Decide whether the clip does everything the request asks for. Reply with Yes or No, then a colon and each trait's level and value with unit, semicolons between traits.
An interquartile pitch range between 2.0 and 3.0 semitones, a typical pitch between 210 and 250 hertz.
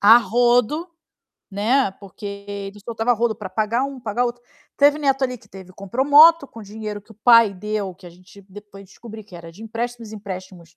No: average, 3.5 semitones; high, 215 Hz